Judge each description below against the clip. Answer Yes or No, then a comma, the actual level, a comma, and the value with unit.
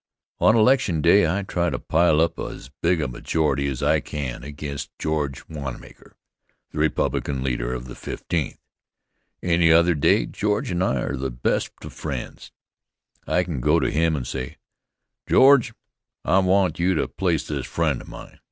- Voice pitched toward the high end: No, very low, 80 Hz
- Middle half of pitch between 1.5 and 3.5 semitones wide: No, average, 4.5 semitones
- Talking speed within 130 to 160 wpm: No, average, 170 wpm